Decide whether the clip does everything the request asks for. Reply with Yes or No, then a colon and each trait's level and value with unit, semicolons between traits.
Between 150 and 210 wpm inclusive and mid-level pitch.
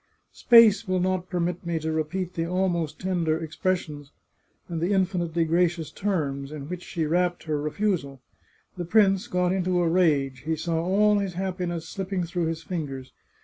Yes: average, 170 wpm; medium, 175 Hz